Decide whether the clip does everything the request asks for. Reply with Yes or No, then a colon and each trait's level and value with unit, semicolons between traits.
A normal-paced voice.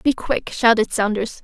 Yes: average, 165 wpm